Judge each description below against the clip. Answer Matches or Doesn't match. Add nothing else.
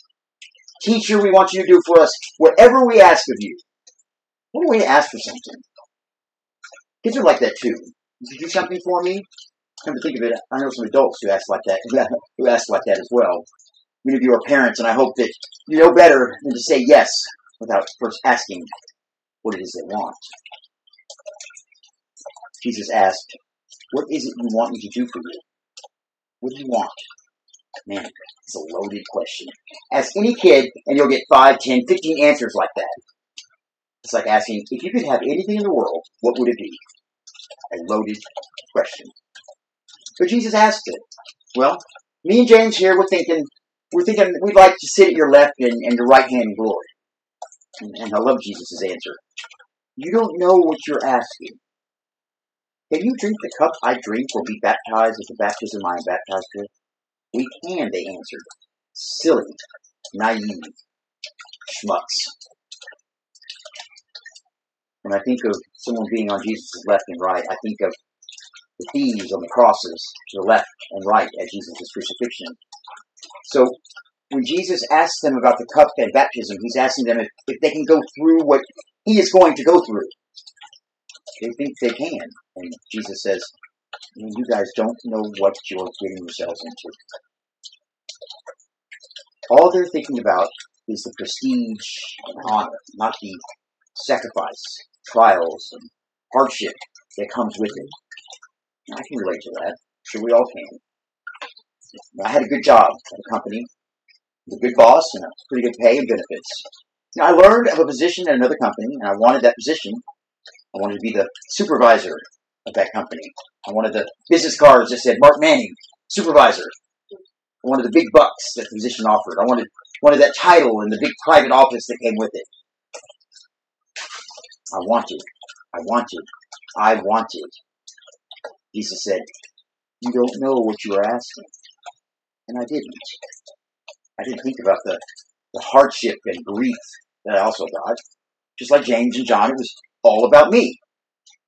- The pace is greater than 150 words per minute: Matches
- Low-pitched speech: Doesn't match